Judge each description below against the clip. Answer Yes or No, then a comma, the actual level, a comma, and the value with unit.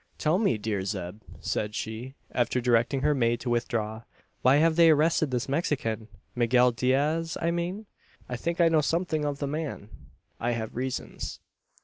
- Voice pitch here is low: Yes, low, 130 Hz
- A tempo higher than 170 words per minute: No, average, 165 wpm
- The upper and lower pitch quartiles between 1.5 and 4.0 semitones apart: No, average, 5.3 semitones